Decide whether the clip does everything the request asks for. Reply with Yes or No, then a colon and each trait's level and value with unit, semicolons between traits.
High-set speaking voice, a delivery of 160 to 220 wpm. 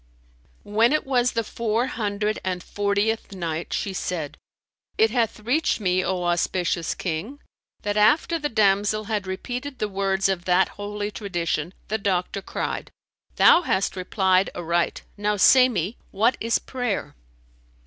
No: high, 205 Hz; average, 145 wpm